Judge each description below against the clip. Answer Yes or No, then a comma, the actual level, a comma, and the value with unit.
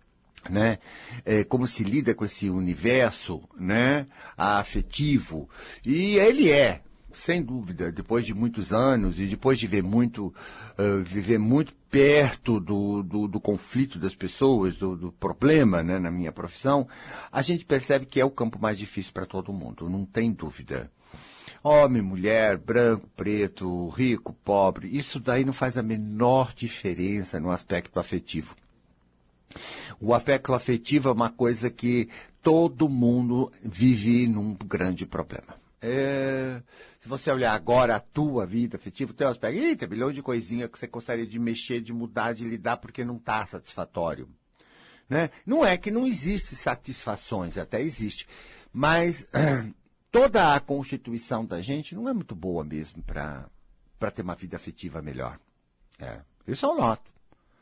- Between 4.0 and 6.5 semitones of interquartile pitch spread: Yes, wide, 5.4 semitones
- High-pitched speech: No, low, 115 Hz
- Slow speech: No, average, 150 wpm